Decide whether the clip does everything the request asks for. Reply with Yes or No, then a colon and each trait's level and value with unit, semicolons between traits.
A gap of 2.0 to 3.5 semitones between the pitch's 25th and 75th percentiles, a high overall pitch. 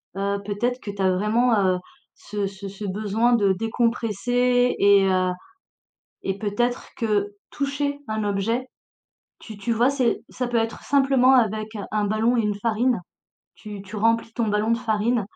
Yes: average, 3.1 semitones; high, 220 Hz